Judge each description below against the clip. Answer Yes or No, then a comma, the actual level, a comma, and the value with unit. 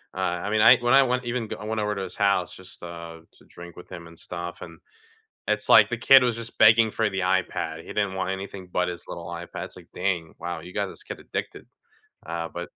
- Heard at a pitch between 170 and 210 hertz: No, very low, 95 Hz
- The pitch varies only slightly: No, average, 3.9 semitones